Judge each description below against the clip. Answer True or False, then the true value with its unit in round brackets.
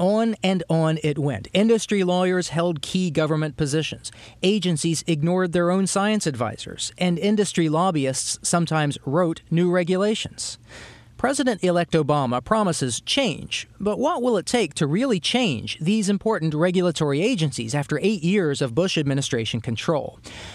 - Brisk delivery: False (140 wpm)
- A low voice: False (170 Hz)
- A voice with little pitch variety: False (5.1 semitones)